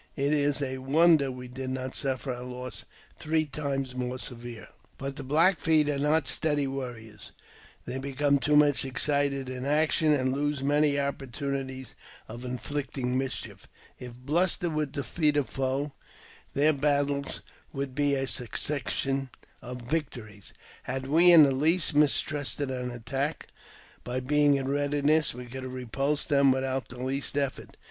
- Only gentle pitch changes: Yes, narrow, 2.2 semitones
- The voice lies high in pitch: No, medium, 140 Hz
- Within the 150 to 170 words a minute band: Yes, average, 155 wpm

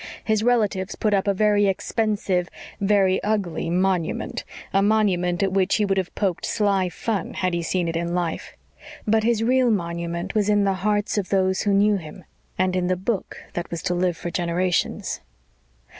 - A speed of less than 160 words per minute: No, average, 185 wpm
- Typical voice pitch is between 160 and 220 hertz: Yes, high, 190 Hz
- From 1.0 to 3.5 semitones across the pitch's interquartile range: Yes, average, 2.7 semitones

